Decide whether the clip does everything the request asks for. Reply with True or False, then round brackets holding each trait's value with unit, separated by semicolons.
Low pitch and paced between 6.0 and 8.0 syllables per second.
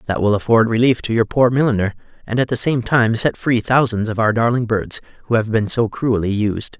False (115 Hz; 5.5 syllables/s)